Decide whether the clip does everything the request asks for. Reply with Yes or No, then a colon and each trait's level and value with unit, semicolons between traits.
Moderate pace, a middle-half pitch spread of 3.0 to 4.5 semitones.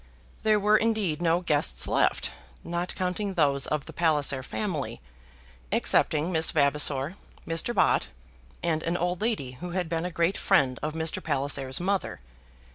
Yes: average, 150 wpm; average, 3.8 semitones